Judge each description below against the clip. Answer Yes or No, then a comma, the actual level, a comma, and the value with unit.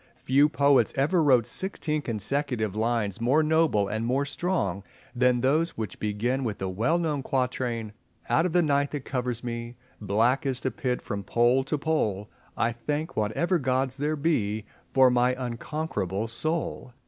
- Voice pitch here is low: Yes, low, 125 Hz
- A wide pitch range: No, average, 4.4 semitones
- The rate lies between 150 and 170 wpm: Yes, average, 160 wpm